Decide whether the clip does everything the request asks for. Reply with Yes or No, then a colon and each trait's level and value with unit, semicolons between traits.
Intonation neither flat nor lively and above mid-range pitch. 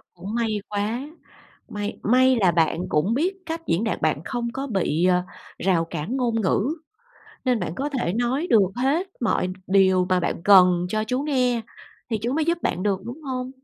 No: wide, 5.7 semitones; high, 220 Hz